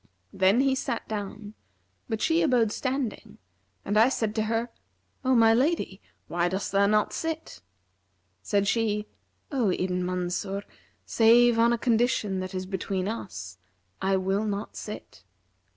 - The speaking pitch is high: Yes, high, 215 Hz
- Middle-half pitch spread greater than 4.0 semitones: No, average, 3.7 semitones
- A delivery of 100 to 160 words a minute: Yes, average, 150 wpm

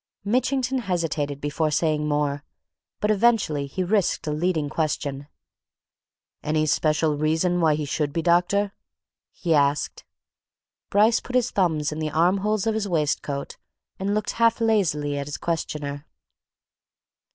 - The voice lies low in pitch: No, medium, 160 Hz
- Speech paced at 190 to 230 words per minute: No, slow, 135 wpm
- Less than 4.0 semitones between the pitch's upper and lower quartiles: No, average, 5.3 semitones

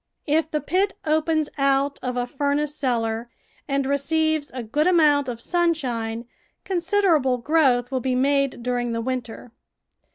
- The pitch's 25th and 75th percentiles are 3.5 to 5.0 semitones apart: Yes, average, 4.0 semitones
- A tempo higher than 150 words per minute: No, average, 140 wpm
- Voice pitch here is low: No, very high, 275 Hz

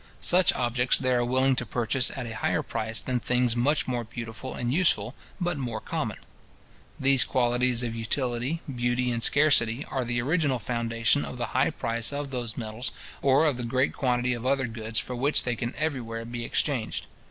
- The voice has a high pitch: No, low, 125 Hz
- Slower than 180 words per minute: No, average, 185 wpm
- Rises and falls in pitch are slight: Yes, narrow, 2.2 semitones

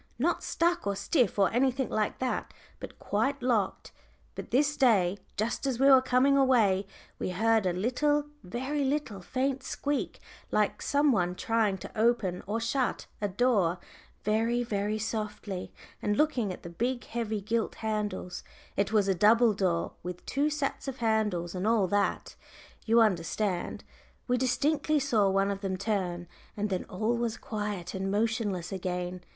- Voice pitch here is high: Yes, high, 220 Hz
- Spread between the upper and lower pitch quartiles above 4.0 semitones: Yes, average, 4.6 semitones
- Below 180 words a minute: Yes, average, 160 wpm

